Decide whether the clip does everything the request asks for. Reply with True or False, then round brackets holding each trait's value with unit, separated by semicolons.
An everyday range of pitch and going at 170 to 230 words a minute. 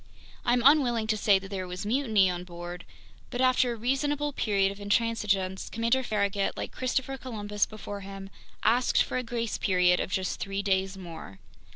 True (4.1 semitones; 175 wpm)